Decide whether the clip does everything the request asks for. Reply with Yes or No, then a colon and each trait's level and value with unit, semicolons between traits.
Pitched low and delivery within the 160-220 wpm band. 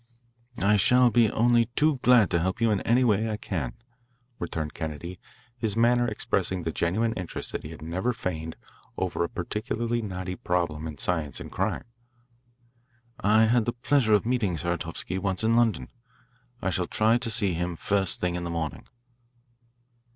Yes: low, 100 Hz; average, 170 wpm